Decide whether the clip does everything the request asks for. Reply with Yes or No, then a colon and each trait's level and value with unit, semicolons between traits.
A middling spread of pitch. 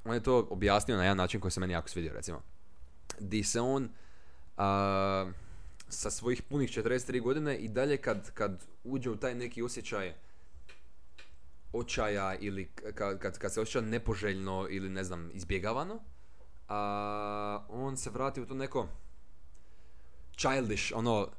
No: wide, 6.2 semitones